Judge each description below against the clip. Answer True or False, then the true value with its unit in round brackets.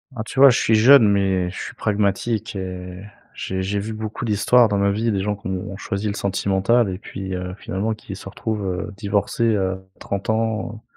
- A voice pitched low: True (100 Hz)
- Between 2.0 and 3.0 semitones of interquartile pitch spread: True (2.4 semitones)